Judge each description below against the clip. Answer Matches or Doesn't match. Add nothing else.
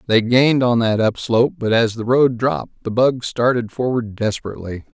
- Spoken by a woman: Doesn't match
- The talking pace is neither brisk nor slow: Matches